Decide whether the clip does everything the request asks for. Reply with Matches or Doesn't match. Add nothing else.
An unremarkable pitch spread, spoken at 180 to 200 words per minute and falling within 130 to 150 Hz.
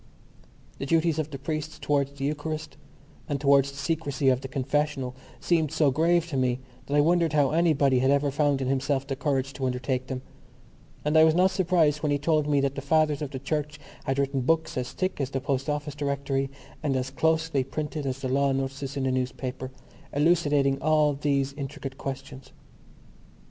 Doesn't match